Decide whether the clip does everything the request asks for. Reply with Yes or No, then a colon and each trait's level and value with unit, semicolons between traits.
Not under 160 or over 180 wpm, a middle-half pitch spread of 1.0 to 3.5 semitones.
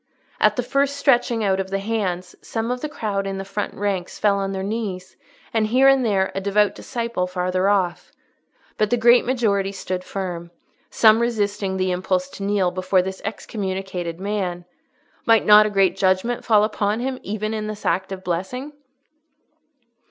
Yes: average, 175 wpm; average, 2.9 semitones